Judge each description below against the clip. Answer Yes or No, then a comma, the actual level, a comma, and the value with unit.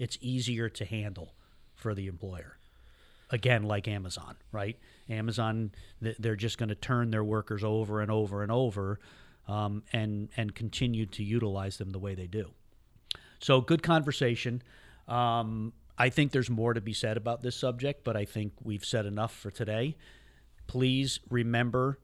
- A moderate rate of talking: Yes, average, 160 wpm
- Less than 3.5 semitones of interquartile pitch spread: Yes, average, 2.8 semitones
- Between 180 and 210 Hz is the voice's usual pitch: No, low, 110 Hz